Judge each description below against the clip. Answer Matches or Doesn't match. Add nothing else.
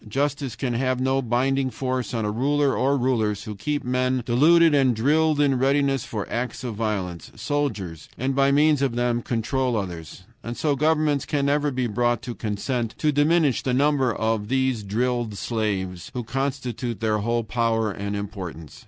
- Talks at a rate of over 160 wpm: Matches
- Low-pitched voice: Matches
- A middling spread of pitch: Matches